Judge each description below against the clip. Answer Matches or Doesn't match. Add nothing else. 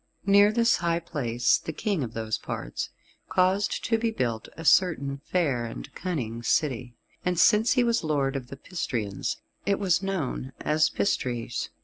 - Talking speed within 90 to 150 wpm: Doesn't match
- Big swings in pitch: Matches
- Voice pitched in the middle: Matches